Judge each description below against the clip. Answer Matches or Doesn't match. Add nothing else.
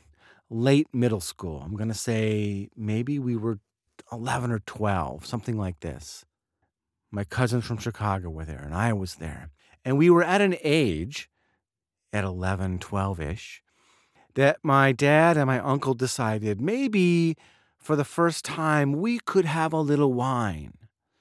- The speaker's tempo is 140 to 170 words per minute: Matches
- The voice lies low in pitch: Matches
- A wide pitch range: Matches